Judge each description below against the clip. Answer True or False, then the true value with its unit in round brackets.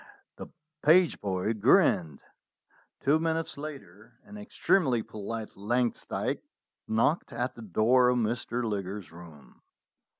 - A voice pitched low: True (115 Hz)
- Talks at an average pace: False (110 wpm)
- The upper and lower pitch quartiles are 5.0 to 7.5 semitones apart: True (5.4 semitones)